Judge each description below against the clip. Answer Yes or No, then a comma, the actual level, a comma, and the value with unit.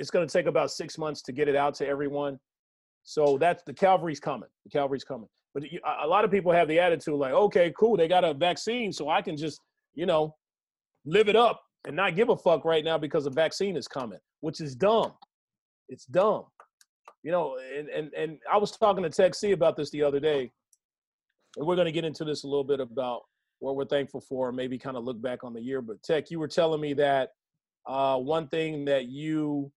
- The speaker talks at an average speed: No, fast, 230 wpm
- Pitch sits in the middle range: Yes, medium, 155 Hz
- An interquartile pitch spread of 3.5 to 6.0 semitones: Yes, average, 4.0 semitones